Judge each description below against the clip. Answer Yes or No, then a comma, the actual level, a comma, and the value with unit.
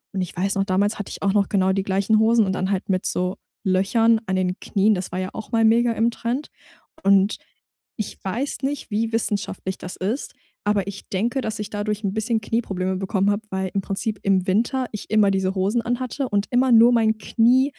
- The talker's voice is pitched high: Yes, high, 205 Hz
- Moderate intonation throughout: Yes, average, 3.1 semitones